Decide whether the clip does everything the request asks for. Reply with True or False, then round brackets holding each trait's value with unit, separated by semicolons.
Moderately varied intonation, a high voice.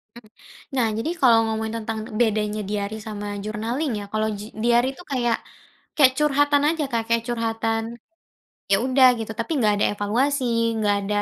True (3.2 semitones; 225 Hz)